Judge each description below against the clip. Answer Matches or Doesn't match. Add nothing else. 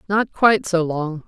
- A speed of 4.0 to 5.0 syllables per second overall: Matches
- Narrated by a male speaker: Doesn't match